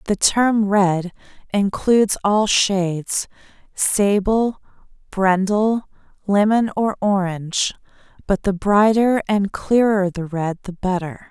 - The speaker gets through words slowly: Yes, slow, 105 wpm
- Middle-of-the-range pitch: No, high, 200 Hz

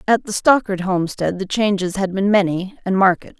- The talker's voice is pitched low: No, high, 195 Hz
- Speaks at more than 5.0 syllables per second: Yes, 5.4 syllables/s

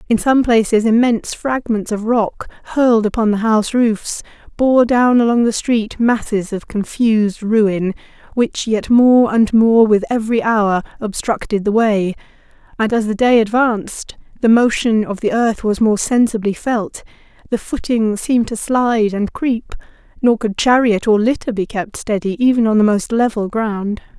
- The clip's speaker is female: Yes, female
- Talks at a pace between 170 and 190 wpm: No, average, 160 wpm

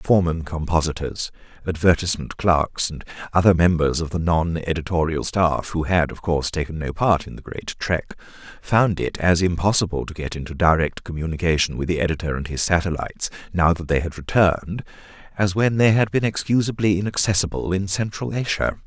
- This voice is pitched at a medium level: No, very low, 90 Hz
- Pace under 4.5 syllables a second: No, 5.6 syllables/s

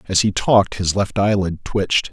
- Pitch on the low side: Yes, low, 100 Hz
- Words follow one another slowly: No, average, 200 wpm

